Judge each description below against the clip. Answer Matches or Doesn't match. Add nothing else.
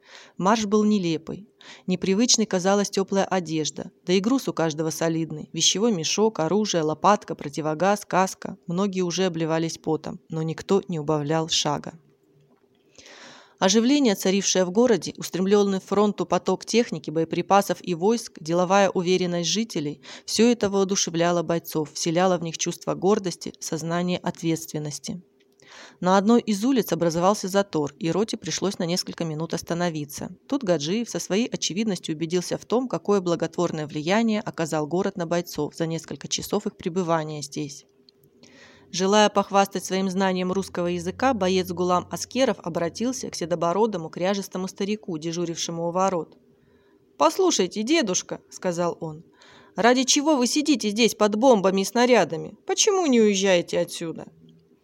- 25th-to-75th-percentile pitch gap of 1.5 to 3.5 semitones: Doesn't match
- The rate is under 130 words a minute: Doesn't match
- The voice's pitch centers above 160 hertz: Matches